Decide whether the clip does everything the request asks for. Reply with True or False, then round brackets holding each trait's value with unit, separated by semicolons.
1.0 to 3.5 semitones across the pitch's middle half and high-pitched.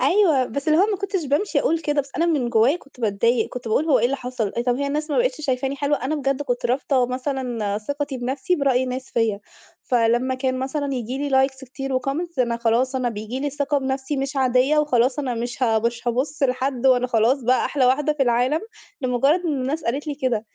True (2.9 semitones; 265 Hz)